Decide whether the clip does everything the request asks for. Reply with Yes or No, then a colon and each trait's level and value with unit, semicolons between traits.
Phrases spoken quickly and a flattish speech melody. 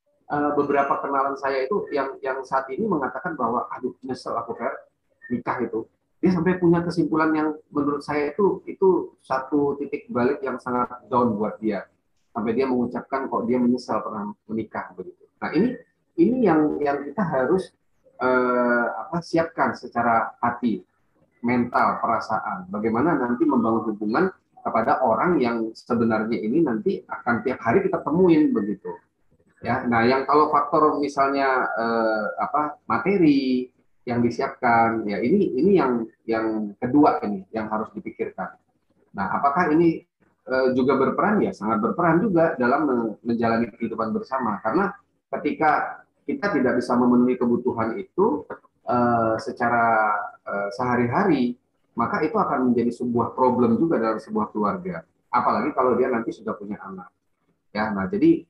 No: fast, 145 wpm; average, 4.0 semitones